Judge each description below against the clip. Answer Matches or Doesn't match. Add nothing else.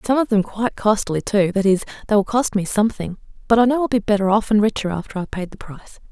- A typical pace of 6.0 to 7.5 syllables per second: Matches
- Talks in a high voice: Matches